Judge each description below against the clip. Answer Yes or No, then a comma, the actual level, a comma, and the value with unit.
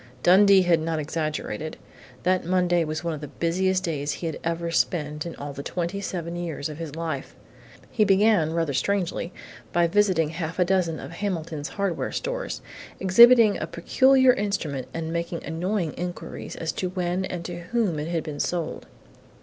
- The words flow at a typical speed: Yes, average, 175 wpm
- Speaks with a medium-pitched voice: Yes, medium, 170 Hz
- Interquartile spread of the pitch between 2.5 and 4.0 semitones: Yes, average, 2.8 semitones